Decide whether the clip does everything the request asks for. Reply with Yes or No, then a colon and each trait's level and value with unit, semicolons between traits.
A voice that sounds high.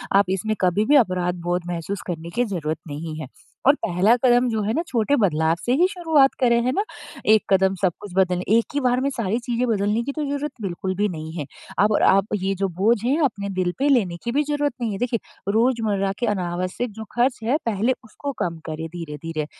Yes: high, 210 Hz